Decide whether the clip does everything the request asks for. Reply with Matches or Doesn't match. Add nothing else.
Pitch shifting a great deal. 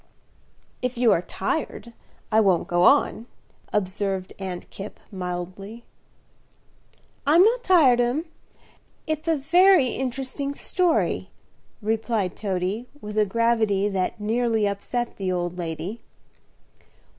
Doesn't match